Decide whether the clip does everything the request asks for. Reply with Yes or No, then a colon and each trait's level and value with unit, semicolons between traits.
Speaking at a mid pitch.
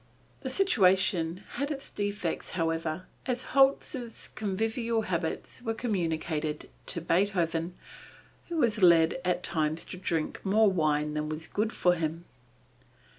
Yes: medium, 180 Hz